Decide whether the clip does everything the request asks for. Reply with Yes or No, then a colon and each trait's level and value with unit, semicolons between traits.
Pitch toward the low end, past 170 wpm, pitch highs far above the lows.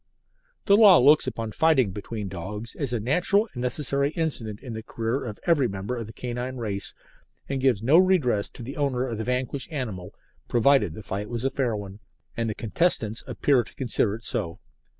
No: low, 120 Hz; average, 195 wpm; average, 4.4 semitones